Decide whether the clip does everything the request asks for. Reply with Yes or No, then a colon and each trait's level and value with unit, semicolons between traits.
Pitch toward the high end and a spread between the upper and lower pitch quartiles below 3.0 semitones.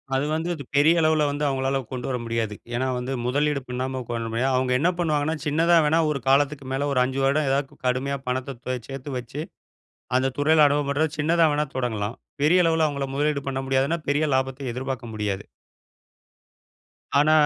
No: medium, 140 Hz; narrow, 2.6 semitones